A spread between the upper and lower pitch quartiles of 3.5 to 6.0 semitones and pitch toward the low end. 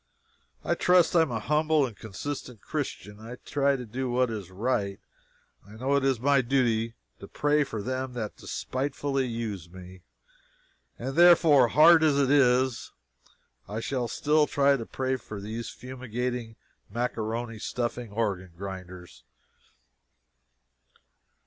Yes: average, 4.1 semitones; low, 125 Hz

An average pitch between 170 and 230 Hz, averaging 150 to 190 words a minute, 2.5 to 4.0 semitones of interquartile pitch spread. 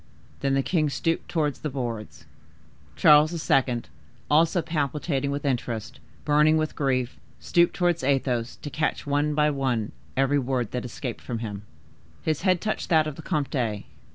No: medium, 140 Hz; average, 155 wpm; average, 3.5 semitones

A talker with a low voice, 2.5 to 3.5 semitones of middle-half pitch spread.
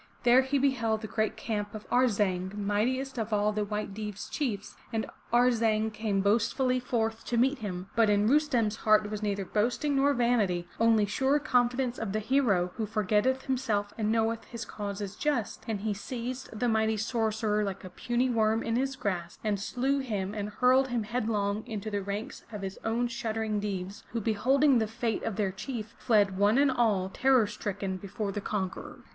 No: high, 220 Hz; average, 3.0 semitones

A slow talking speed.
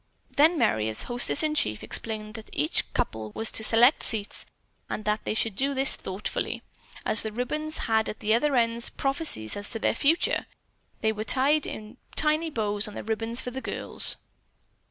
No: average, 175 wpm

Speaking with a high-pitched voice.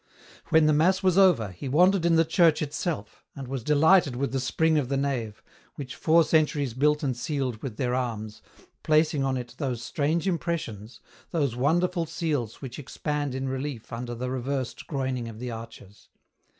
No: medium, 140 Hz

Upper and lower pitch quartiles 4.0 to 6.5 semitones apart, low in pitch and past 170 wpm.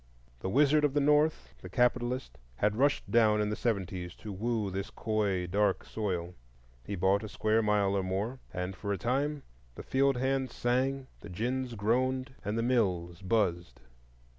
No: average, 5.0 semitones; low, 110 Hz; average, 165 wpm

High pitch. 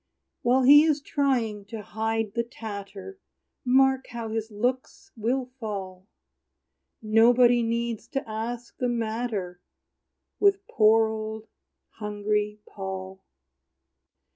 Yes: high, 225 Hz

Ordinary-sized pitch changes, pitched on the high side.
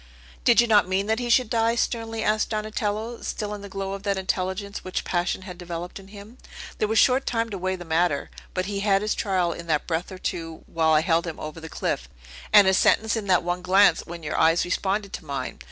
Yes: average, 3.4 semitones; high, 195 Hz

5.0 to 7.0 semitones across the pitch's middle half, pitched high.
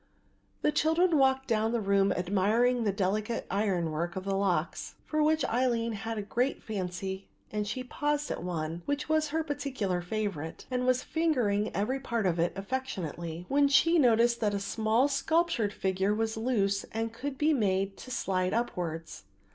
Yes: average, 5.3 semitones; high, 220 Hz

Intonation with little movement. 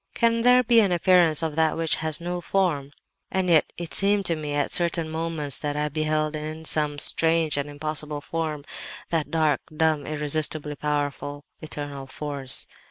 Yes: narrow, 2.2 semitones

